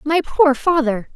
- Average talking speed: Yes, average, 155 wpm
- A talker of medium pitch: No, very high, 285 Hz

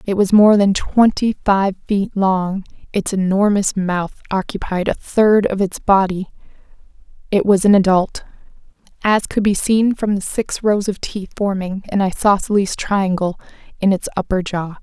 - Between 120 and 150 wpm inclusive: No, average, 160 wpm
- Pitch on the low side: No, high, 195 Hz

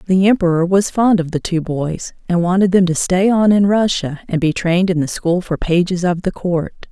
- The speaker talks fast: Yes, fast, 235 wpm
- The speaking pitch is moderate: Yes, medium, 180 Hz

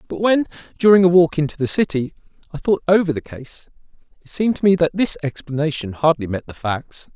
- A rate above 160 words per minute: Yes, average, 200 wpm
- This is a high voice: No, medium, 160 Hz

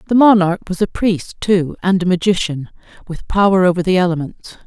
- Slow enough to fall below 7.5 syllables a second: Yes, 5.4 syllables/s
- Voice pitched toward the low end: No, medium, 185 Hz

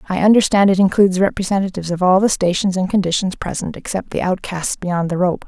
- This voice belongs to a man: No, female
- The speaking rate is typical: Yes, average, 195 wpm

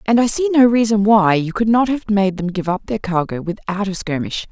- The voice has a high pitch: Yes, high, 205 Hz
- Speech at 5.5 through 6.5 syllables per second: No, 5.3 syllables/s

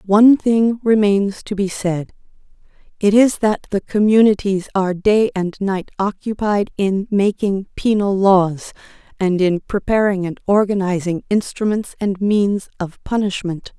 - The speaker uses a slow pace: Yes, slow, 130 wpm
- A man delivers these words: No, female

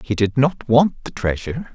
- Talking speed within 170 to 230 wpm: Yes, fast, 205 wpm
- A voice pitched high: No, low, 125 Hz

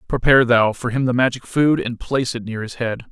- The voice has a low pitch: Yes, low, 120 Hz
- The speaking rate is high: Yes, fast, 250 wpm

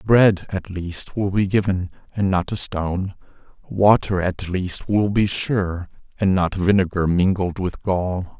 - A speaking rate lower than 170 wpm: Yes, average, 155 wpm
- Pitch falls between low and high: No, very low, 95 Hz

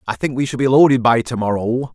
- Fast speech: Yes, fast, 280 wpm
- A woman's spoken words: No, male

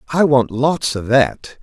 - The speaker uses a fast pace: No, average, 185 wpm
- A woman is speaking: No, male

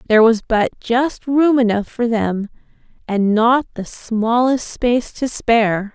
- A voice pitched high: Yes, high, 230 Hz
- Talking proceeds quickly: No, average, 150 wpm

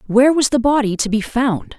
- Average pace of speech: No, fast, 235 wpm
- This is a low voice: No, high, 245 Hz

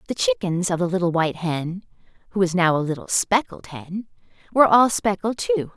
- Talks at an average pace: Yes, average, 190 wpm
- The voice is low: No, medium, 185 Hz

